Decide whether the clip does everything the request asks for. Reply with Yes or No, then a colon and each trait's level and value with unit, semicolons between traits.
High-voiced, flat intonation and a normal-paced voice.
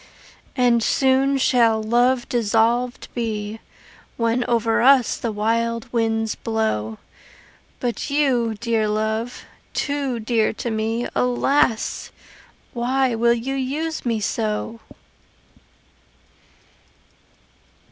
No: high, 235 Hz; narrow, 2.1 semitones; slow, 95 wpm